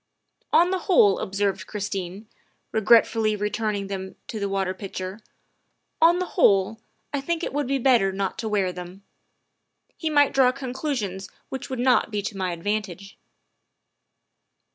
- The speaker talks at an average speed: Yes, average, 160 wpm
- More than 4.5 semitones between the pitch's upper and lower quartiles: Yes, average, 5.0 semitones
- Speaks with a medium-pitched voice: No, high, 210 Hz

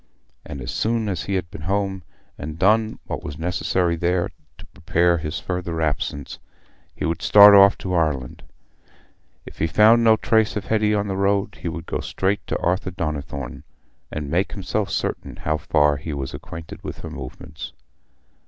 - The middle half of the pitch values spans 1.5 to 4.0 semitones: No, average, 4.5 semitones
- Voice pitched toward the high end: No, very low, 90 Hz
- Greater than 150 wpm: Yes, average, 180 wpm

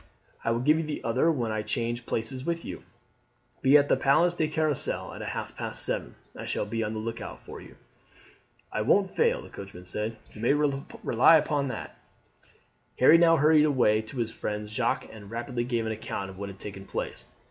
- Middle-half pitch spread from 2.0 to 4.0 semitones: No, wide, 5.6 semitones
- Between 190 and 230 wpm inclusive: Yes, fast, 205 wpm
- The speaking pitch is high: No, low, 120 Hz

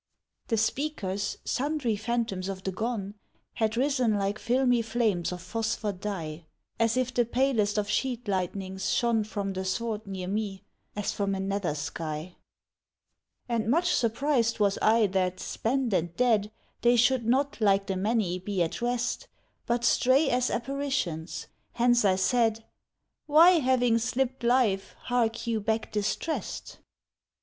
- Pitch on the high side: Yes, high, 225 Hz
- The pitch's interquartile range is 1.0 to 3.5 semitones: No, average, 4.0 semitones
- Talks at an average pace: Yes, average, 145 wpm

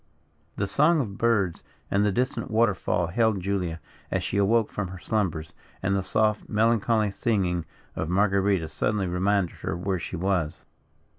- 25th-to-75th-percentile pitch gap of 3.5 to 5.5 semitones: No, average, 3.1 semitones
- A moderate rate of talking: Yes, average, 160 wpm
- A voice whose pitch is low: Yes, low, 100 Hz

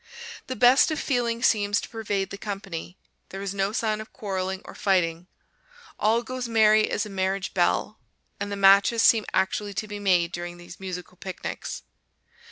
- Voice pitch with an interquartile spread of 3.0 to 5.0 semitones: No, narrow, 2.5 semitones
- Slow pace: No, average, 175 wpm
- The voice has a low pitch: No, high, 200 Hz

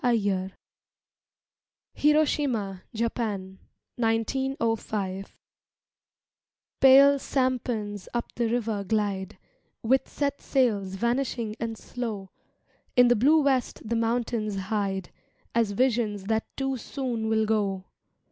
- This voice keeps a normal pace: No, slow, 100 wpm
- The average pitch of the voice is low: No, high, 225 Hz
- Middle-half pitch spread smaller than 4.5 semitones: Yes, average, 3.6 semitones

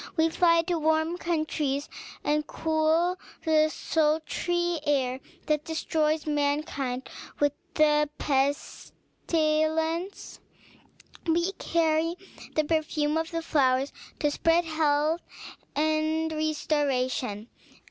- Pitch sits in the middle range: No, very high, 310 Hz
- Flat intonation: Yes, narrow, 1.7 semitones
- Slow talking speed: Yes, slow, 95 wpm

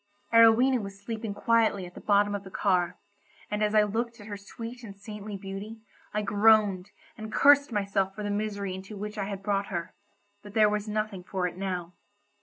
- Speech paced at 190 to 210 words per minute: Yes, average, 200 wpm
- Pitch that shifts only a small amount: Yes, narrow, 1.7 semitones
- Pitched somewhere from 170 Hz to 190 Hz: No, high, 205 Hz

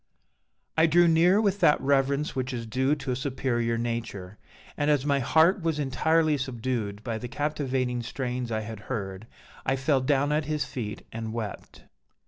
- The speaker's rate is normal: Yes, average, 170 wpm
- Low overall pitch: Yes, low, 130 Hz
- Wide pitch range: No, average, 4.2 semitones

